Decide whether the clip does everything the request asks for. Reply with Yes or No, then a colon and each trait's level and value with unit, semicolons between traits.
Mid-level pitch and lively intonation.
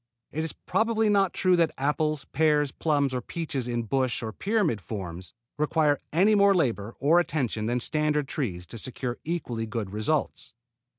Yes: medium, 145 Hz; wide, 5.7 semitones